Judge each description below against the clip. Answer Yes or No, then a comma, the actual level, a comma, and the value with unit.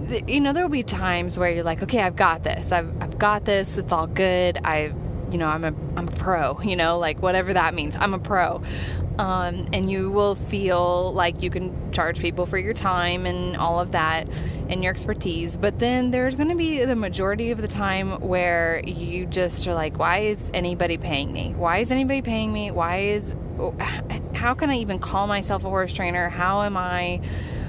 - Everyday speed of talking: No, fast, 210 wpm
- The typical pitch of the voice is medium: Yes, medium, 180 Hz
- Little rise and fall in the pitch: No, average, 4.6 semitones